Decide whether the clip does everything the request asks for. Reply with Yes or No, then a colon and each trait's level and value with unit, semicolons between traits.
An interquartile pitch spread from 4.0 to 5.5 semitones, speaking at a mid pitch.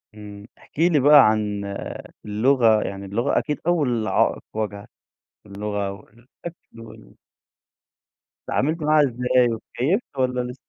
No: average, 5.1 semitones; low, 120 Hz